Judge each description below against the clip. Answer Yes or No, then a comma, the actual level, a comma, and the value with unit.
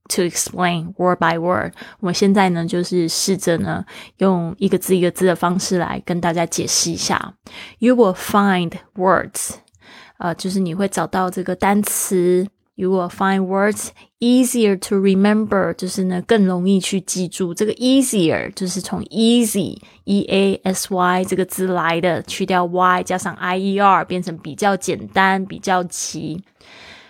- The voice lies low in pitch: No, medium, 185 Hz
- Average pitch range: No, narrow, 1.8 semitones